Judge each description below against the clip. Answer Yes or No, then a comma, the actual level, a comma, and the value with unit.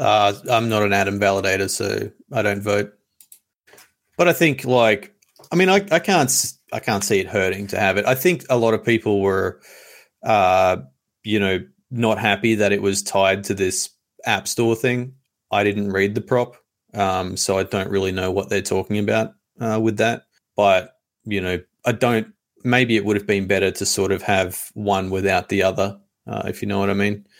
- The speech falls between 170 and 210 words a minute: Yes, average, 200 wpm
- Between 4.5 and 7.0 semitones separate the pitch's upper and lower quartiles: No, average, 2.8 semitones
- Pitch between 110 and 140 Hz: No, low, 100 Hz